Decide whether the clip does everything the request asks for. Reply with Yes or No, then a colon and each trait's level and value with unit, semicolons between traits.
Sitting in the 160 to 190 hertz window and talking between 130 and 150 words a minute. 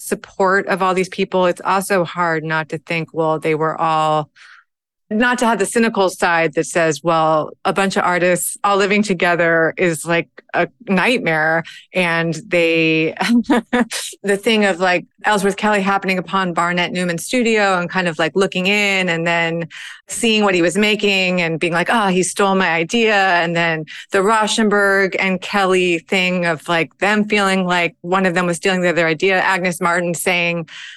No: medium, 185 Hz; average, 180 wpm